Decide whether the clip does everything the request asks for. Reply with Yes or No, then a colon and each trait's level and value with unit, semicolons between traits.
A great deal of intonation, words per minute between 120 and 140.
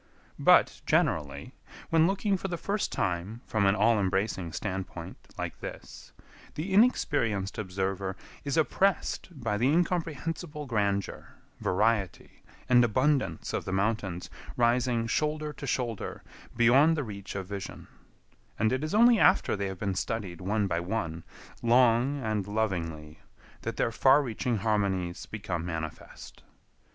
Yes: wide, 6.5 semitones; slow, 135 wpm